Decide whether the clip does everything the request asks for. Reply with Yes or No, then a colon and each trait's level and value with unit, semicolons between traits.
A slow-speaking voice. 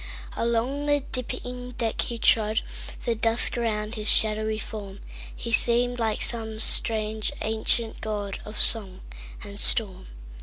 Yes: slow, 115 wpm